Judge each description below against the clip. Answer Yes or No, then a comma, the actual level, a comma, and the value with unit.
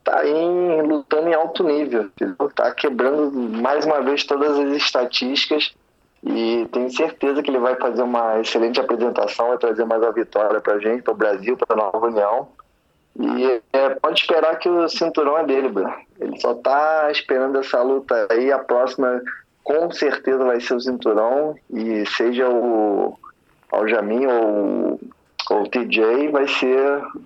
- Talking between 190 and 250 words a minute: No, average, 160 wpm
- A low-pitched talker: Yes, low, 130 Hz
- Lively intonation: No, average, 4.0 semitones